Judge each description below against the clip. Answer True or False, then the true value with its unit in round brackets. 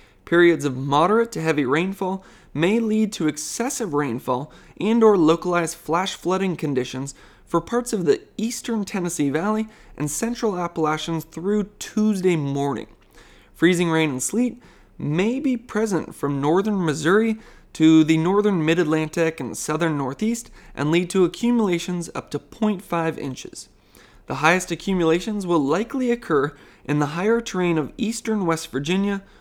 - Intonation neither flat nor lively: False (5.7 semitones)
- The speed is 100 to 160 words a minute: True (140 wpm)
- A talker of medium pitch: True (175 Hz)